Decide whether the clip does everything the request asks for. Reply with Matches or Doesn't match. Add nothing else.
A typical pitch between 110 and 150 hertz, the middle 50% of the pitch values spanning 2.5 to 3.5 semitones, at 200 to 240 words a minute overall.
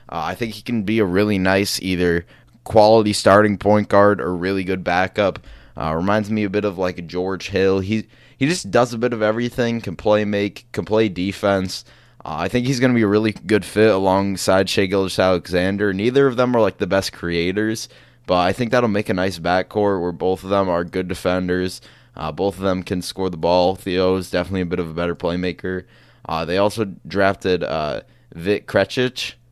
Doesn't match